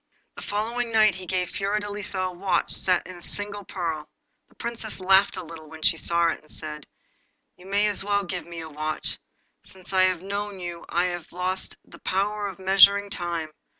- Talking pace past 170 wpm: Yes, average, 195 wpm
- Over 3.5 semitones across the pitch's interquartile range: No, average, 2.9 semitones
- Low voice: No, medium, 185 Hz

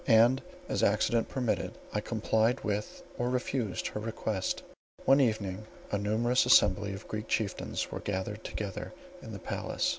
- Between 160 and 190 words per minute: No, average, 150 wpm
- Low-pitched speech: Yes, low, 110 Hz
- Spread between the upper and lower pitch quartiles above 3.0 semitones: No, narrow, 2.6 semitones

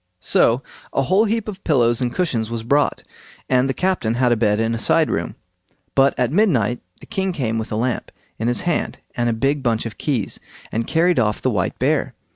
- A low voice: Yes, low, 125 Hz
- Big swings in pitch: Yes, wide, 6.0 semitones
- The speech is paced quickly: Yes, fast, 215 wpm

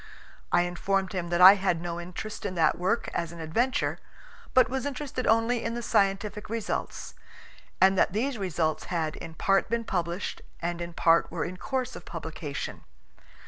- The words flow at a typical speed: Yes, average, 175 wpm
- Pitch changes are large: No, average, 4.8 semitones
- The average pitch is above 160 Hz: Yes, high, 190 Hz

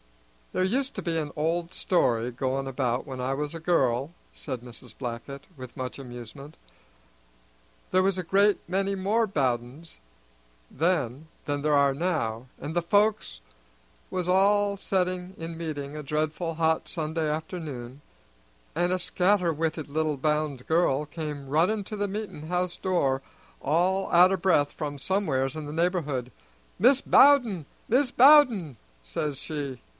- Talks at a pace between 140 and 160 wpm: Yes, average, 150 wpm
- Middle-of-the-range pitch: Yes, medium, 160 Hz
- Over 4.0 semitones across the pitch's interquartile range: Yes, average, 5.0 semitones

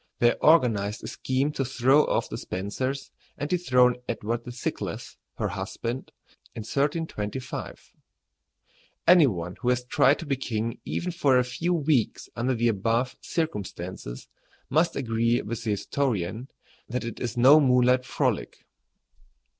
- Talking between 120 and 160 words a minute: Yes, average, 140 wpm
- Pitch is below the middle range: Yes, low, 125 Hz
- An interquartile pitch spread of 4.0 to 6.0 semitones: No, average, 3.4 semitones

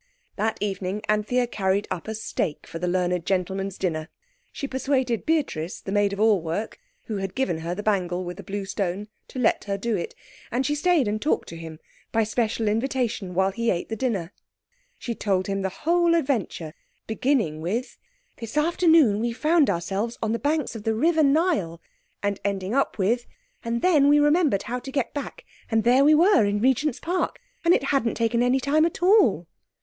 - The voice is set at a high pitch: Yes, high, 220 Hz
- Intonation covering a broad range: Yes, wide, 6.2 semitones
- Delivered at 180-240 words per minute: Yes, average, 195 wpm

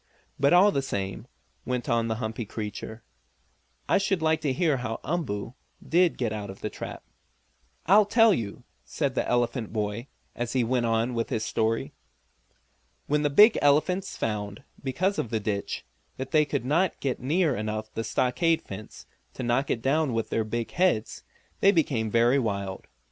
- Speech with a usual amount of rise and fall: No, wide, 5.8 semitones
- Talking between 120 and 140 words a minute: No, average, 175 wpm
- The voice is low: Yes, low, 125 Hz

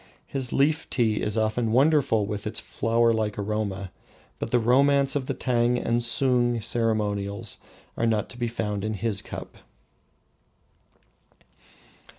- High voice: No, low, 115 Hz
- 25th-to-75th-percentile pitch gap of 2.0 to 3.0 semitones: Yes, narrow, 2.5 semitones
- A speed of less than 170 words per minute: Yes, average, 140 wpm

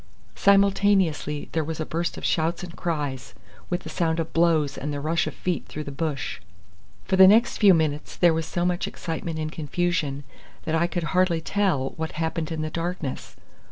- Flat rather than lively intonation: Yes, narrow, 2.3 semitones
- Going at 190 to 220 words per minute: Yes, average, 195 wpm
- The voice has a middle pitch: Yes, medium, 165 Hz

